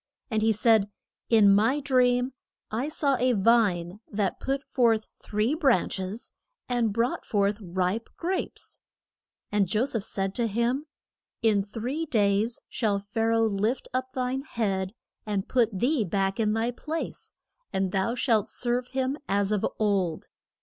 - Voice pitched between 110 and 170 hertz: No, high, 225 Hz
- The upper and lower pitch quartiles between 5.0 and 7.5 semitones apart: No, average, 3.8 semitones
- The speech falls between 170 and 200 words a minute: No, average, 155 wpm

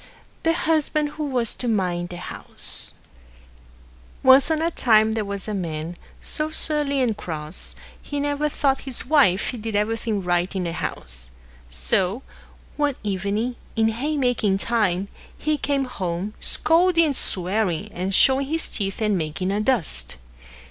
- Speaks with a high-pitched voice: Yes, high, 220 Hz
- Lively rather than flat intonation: Yes, wide, 7.1 semitones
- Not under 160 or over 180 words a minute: No, average, 150 wpm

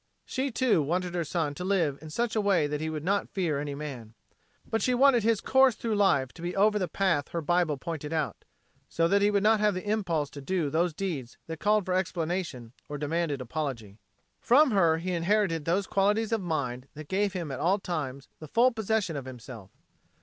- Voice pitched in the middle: Yes, medium, 170 Hz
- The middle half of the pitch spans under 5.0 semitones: No, wide, 5.5 semitones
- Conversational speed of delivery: No, fast, 215 wpm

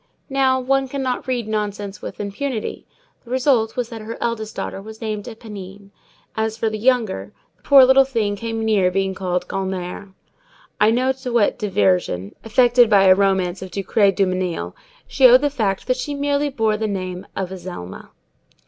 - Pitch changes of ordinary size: Yes, average, 4.5 semitones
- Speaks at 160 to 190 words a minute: Yes, average, 175 wpm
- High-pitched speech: Yes, high, 215 Hz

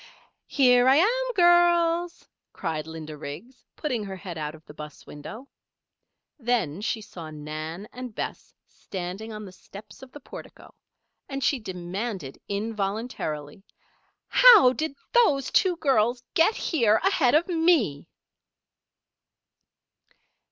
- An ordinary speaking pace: No, slow, 125 wpm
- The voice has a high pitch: Yes, high, 225 Hz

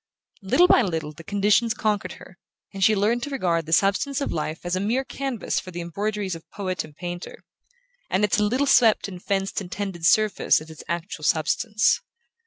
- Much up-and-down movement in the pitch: No, average, 3.8 semitones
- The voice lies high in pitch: Yes, high, 195 Hz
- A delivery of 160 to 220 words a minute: Yes, average, 195 wpm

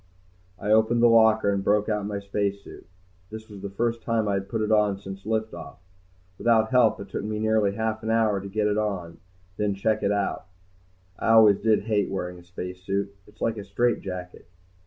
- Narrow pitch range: Yes, narrow, 2.0 semitones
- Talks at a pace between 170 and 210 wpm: Yes, fast, 205 wpm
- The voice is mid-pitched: No, low, 105 Hz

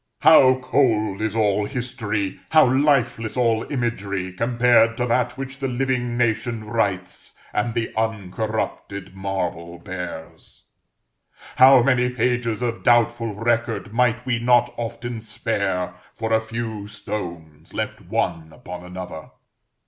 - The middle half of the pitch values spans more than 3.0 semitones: Yes, average, 3.5 semitones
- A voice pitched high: No, low, 115 Hz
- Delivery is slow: Yes, slow, 125 wpm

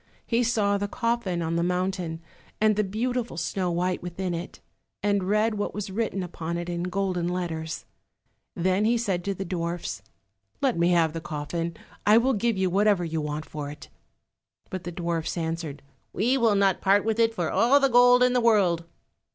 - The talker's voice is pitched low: No, medium, 185 Hz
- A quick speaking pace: No, average, 190 wpm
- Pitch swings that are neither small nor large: Yes, average, 4.1 semitones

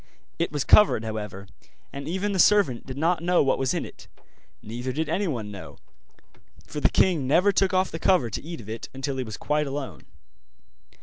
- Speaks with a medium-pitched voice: Yes, medium, 145 Hz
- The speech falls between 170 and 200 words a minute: Yes, average, 195 wpm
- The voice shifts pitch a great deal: Yes, wide, 6.5 semitones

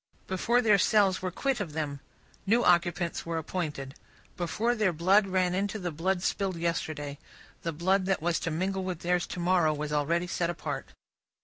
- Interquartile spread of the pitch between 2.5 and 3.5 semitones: Yes, average, 2.8 semitones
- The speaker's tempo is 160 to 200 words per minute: Yes, average, 180 wpm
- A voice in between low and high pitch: Yes, medium, 175 Hz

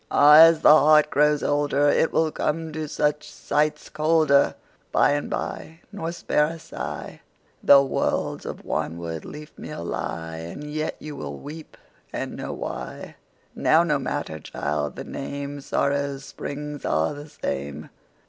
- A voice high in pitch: No, medium, 145 Hz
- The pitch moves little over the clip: Yes, narrow, 1.8 semitones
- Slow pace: Yes, slow, 130 wpm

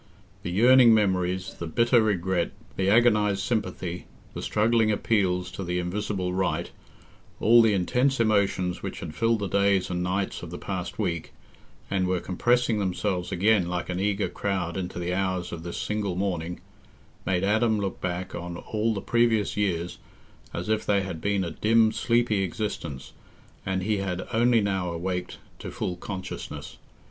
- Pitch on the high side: No, very low, 95 Hz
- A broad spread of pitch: No, average, 3.1 semitones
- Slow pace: No, average, 160 wpm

